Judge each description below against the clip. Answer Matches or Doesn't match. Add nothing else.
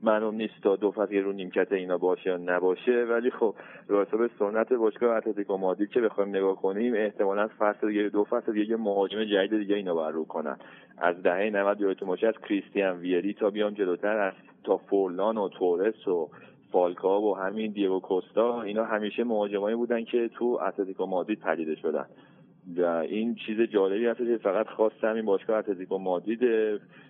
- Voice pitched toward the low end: Matches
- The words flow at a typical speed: Doesn't match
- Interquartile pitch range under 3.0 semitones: Matches